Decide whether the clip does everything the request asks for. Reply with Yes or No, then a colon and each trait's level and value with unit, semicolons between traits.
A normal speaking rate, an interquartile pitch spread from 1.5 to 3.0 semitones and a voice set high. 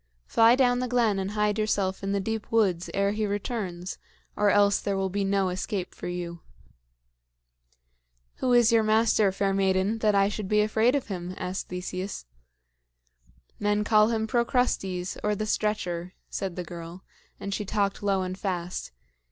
Yes: average, 170 wpm; narrow, 2.4 semitones; high, 200 Hz